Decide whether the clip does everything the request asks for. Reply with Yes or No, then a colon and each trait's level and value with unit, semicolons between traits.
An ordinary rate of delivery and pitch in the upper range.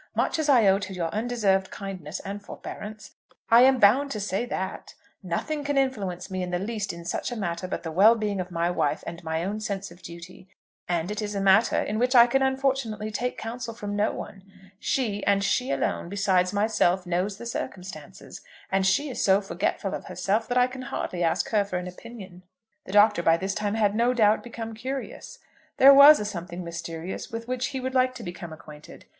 No: fast, 210 wpm; high, 205 Hz